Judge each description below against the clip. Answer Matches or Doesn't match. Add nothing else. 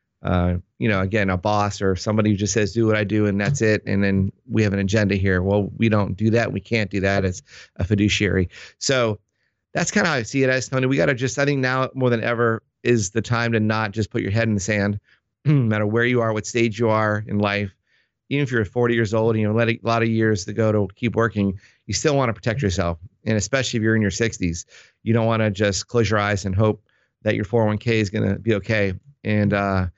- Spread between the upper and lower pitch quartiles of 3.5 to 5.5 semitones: Doesn't match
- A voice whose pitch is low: Matches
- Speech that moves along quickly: Matches